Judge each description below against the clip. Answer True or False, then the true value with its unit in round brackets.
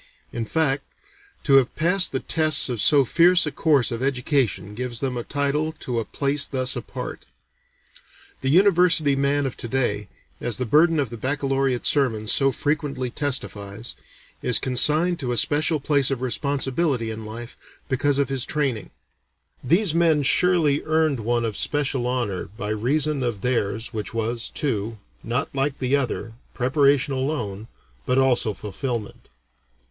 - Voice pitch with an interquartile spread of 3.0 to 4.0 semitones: True (3.7 semitones)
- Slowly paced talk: False (155 wpm)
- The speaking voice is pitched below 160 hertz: True (135 Hz)